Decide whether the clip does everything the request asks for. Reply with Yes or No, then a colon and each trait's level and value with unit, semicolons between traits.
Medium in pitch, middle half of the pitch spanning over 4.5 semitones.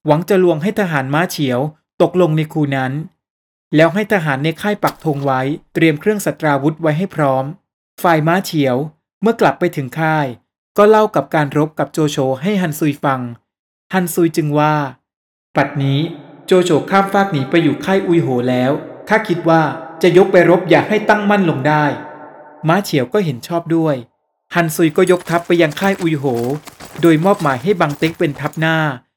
No: medium, 160 Hz; average, 3.3 semitones